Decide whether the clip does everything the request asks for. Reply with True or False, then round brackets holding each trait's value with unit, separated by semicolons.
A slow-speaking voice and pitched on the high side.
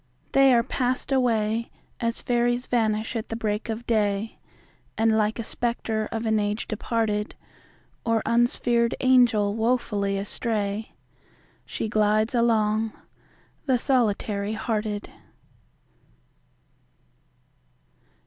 True (100 wpm; 225 Hz)